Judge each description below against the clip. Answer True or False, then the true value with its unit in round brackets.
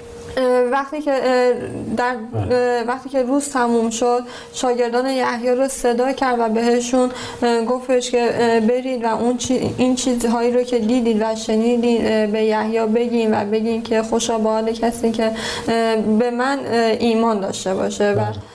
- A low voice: False (240 Hz)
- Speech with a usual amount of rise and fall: False (1.8 semitones)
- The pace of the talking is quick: False (140 wpm)